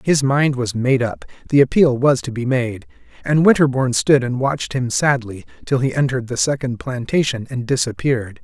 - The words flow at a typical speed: Yes, average, 185 wpm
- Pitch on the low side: Yes, low, 130 Hz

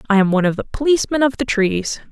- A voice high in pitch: Yes, high, 230 Hz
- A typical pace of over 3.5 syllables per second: Yes, 7.1 syllables/s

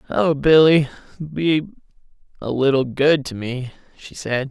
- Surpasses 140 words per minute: No, slow, 135 wpm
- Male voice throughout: Yes, male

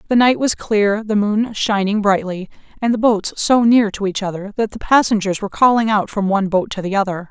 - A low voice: No, high, 210 Hz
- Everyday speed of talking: No, fast, 230 wpm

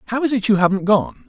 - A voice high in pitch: Yes, high, 200 Hz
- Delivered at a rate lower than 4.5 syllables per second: No, 6.7 syllables/s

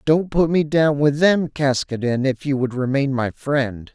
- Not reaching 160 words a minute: No, average, 200 wpm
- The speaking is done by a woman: No, male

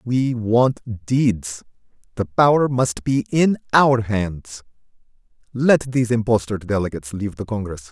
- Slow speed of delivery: Yes, slow, 120 wpm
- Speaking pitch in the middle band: No, low, 115 Hz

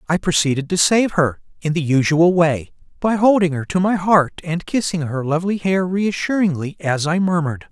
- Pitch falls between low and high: Yes, medium, 170 Hz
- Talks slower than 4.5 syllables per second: No, 5.2 syllables/s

